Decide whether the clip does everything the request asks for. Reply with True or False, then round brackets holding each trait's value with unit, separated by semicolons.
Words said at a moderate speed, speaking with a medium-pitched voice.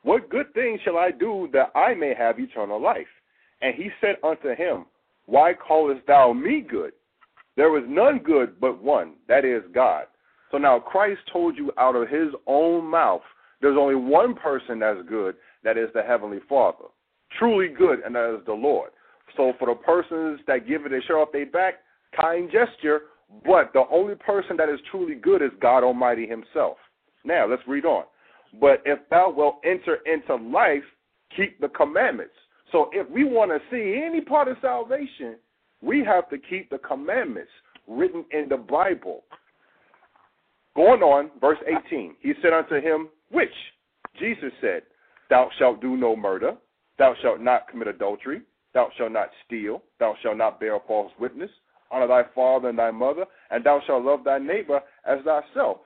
True (175 wpm; 160 Hz)